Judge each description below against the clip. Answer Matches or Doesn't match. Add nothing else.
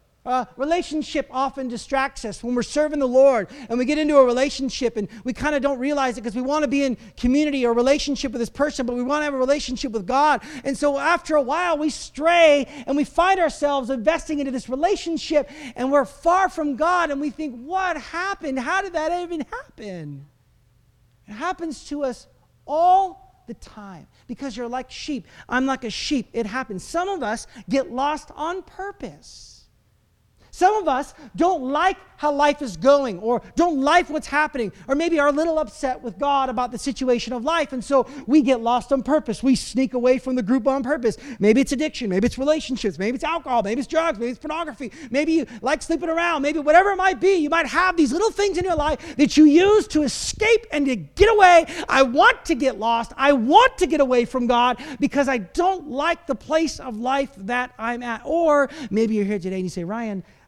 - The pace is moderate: Doesn't match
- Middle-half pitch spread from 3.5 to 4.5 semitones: Matches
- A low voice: Doesn't match